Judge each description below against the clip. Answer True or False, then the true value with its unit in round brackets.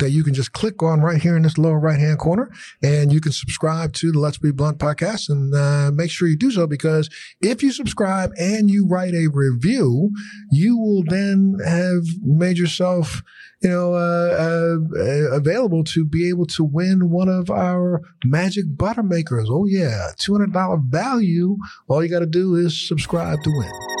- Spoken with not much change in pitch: False (3.3 semitones)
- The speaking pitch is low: False (170 Hz)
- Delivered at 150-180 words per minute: False (195 wpm)